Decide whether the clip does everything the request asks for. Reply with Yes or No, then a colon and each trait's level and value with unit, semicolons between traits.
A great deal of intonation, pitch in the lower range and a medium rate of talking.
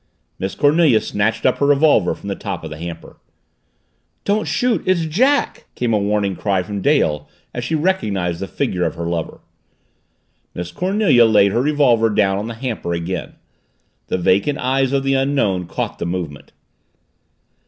Yes: wide, 7.5 semitones; low, 110 Hz; average, 165 wpm